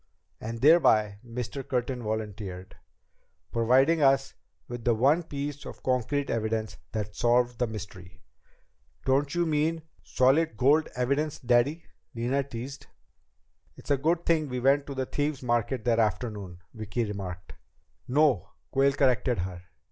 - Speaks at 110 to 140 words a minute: Yes, slow, 135 wpm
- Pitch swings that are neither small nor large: Yes, average, 4.3 semitones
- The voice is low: Yes, low, 125 Hz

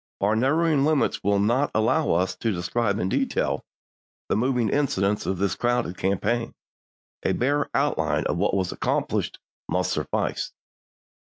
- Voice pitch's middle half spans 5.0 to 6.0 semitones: Yes, wide, 5.5 semitones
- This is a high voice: No, low, 110 Hz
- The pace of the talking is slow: No, average, 150 wpm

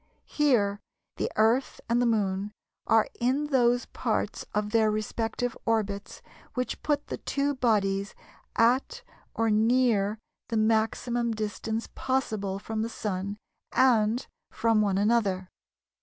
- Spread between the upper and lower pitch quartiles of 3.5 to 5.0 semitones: No, average, 2.7 semitones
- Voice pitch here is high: Yes, high, 225 Hz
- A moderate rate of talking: No, slow, 125 wpm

